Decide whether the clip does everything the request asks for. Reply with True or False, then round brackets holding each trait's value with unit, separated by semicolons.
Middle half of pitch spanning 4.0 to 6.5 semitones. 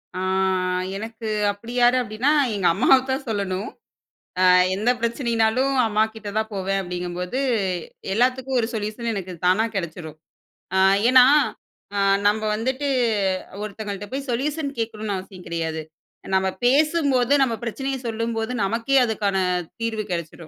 True (4.3 semitones)